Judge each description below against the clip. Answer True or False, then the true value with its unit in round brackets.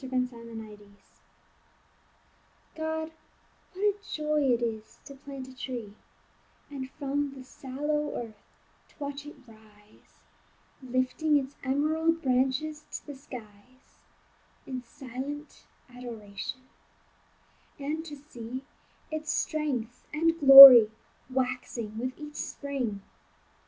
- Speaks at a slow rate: True (110 wpm)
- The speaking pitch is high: True (265 Hz)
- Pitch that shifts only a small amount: False (3.6 semitones)